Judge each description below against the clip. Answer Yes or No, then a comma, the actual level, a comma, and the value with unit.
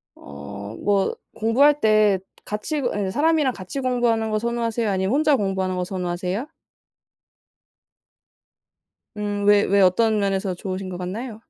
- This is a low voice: No, high, 205 Hz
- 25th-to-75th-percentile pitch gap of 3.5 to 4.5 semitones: Yes, average, 3.8 semitones